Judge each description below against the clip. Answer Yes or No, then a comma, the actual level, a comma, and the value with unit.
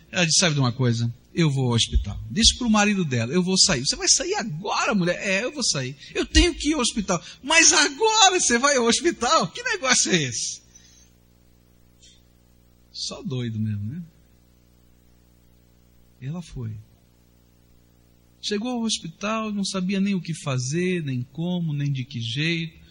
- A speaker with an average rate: Yes, average, 170 wpm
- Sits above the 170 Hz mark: No, low, 135 Hz